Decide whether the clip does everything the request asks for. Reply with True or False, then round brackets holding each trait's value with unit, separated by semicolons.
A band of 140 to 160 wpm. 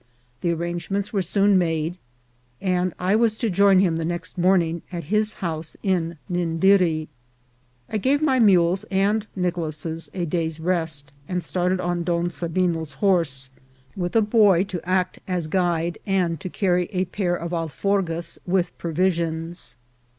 True (150 wpm)